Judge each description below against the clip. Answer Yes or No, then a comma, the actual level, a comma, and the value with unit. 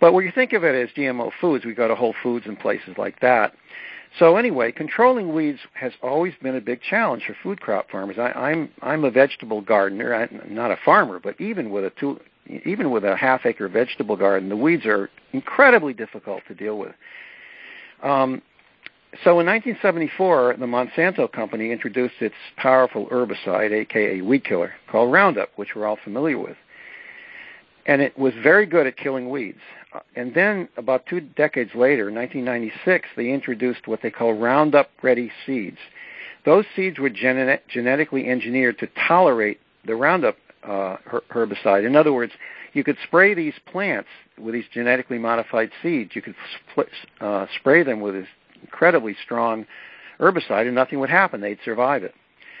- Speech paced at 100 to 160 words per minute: No, average, 170 wpm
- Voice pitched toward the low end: Yes, low, 130 Hz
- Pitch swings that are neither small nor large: No, wide, 6.6 semitones